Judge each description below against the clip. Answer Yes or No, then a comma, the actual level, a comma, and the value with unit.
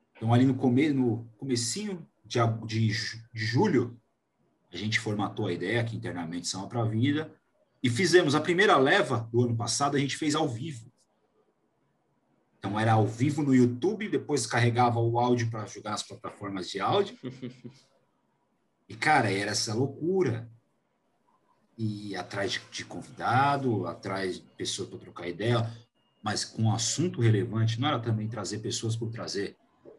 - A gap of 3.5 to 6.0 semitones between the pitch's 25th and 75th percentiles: No, average, 2.9 semitones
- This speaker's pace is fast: No, average, 155 wpm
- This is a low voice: Yes, low, 120 Hz